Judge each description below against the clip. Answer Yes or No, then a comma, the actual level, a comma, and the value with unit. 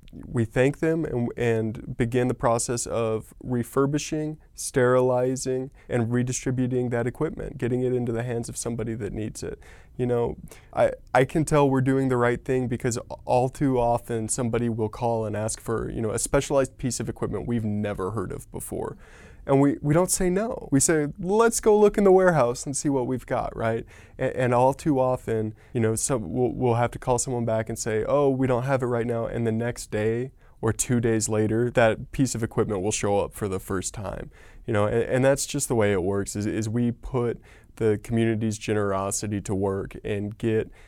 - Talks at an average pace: No, fast, 210 wpm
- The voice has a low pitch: Yes, low, 120 Hz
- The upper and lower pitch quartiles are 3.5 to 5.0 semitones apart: No, average, 2.8 semitones